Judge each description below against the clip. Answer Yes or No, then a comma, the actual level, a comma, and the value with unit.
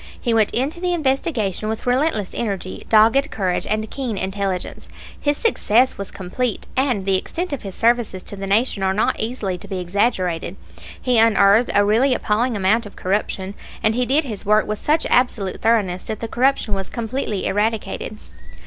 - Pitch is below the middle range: No, high, 220 Hz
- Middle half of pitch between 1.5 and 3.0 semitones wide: No, average, 4.1 semitones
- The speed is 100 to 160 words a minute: No, average, 175 wpm